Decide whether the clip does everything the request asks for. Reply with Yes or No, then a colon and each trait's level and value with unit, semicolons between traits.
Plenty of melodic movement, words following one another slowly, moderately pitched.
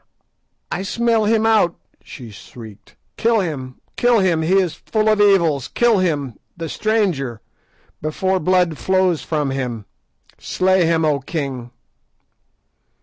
Yes: wide, 6.1 semitones; slow, 130 wpm; medium, 170 Hz